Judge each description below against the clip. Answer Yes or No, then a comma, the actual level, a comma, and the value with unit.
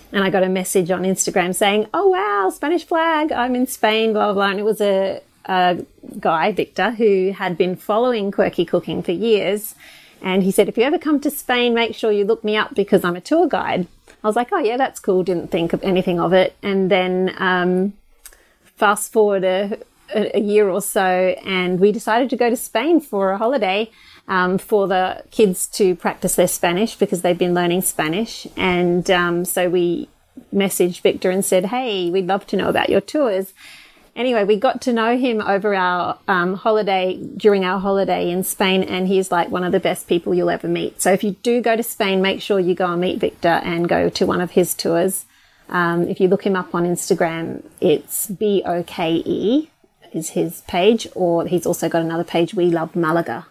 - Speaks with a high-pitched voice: Yes, high, 195 Hz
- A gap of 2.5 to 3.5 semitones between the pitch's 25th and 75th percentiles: Yes, average, 3.2 semitones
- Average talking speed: No, fast, 210 wpm